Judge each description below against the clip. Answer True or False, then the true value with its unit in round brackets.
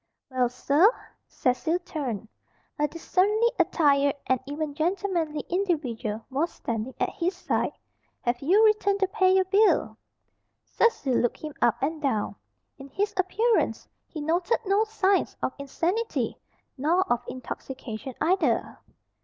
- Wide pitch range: True (6.4 semitones)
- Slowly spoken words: True (130 wpm)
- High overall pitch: True (315 Hz)